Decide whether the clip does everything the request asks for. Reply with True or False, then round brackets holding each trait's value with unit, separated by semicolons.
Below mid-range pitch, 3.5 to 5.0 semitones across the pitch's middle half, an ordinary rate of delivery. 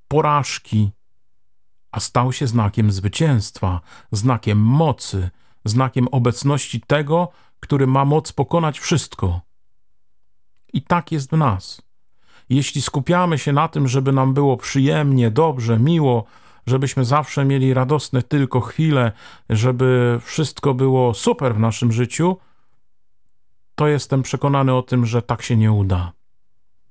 True (130 Hz; 3.9 semitones; 125 wpm)